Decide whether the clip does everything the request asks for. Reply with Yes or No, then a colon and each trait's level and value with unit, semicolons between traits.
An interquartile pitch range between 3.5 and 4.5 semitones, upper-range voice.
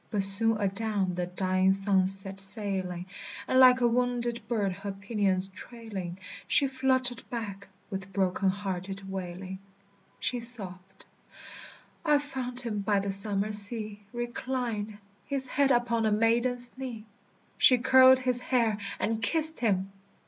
Yes: average, 4.1 semitones; high, 215 Hz